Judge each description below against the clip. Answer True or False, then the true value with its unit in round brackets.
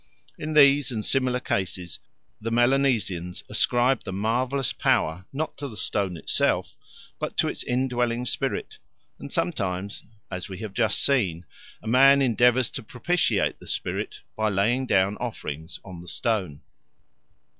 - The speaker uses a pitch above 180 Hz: False (115 Hz)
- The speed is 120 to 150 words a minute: True (145 wpm)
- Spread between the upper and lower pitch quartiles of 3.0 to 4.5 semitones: False (5.4 semitones)